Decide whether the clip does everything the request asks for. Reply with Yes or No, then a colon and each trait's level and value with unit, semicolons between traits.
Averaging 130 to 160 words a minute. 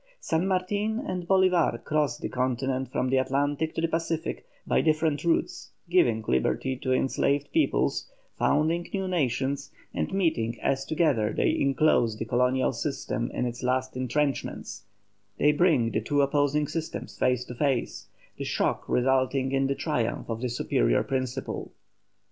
Yes: average, 150 wpm